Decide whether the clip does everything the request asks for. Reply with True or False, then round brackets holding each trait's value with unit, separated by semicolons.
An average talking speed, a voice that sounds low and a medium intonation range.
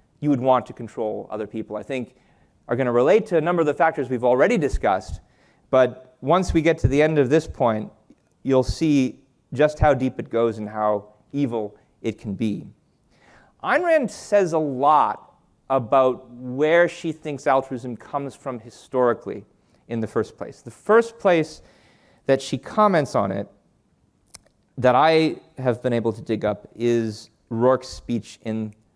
True (170 wpm; 130 Hz; 4.8 semitones)